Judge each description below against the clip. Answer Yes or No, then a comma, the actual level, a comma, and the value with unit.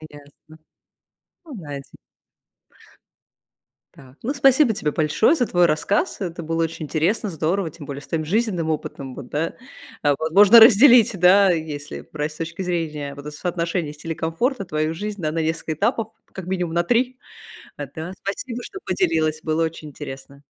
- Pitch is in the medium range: Yes, medium, 165 Hz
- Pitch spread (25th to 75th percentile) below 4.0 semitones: No, average, 4.6 semitones